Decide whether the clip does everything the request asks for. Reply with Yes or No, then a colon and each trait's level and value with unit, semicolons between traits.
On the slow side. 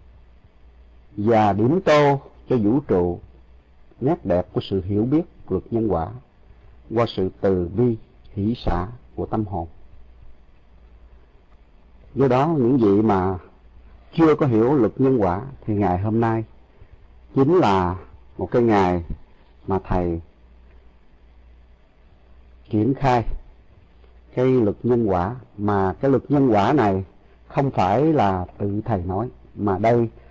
Yes: slow, 130 wpm